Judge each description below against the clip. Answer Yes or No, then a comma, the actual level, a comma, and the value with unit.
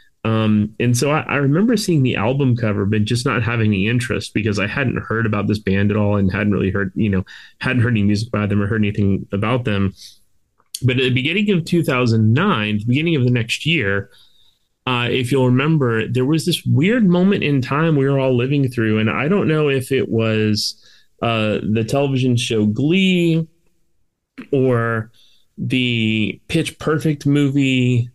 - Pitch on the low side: Yes, low, 120 Hz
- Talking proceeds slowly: No, average, 185 wpm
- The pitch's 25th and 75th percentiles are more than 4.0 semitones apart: Yes, average, 4.8 semitones